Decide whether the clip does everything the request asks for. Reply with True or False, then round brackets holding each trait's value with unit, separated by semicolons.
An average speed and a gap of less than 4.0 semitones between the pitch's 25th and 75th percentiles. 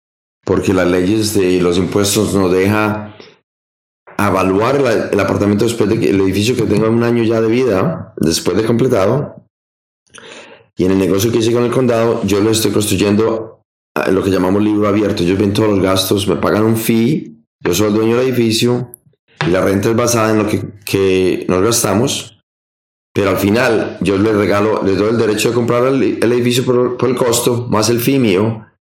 False (195 wpm; 3.3 semitones)